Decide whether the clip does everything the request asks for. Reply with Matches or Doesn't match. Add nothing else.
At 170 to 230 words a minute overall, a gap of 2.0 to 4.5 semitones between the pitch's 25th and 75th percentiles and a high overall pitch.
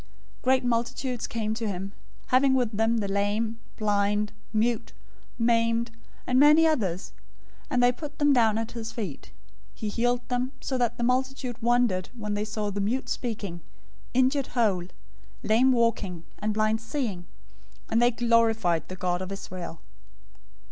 Doesn't match